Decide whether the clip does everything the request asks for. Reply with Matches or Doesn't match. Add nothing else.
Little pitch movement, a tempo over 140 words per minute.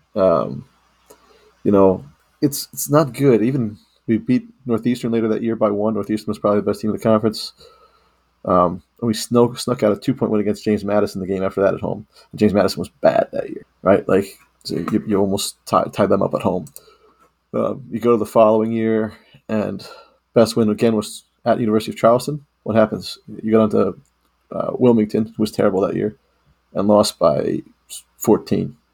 Matches